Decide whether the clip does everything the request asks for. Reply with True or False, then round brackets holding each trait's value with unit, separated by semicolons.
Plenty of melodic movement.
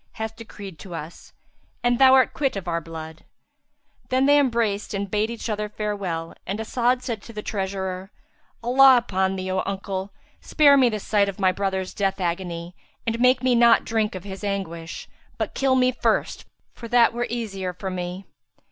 False (4.1 semitones)